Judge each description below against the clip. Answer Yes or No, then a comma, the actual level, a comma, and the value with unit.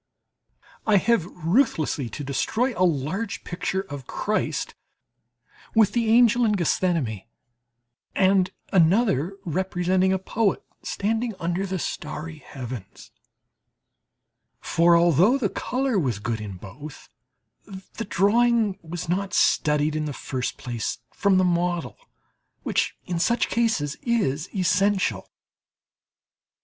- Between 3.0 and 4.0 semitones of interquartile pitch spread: No, wide, 5.4 semitones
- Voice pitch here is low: No, medium, 180 Hz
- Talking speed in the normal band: No, slow, 115 wpm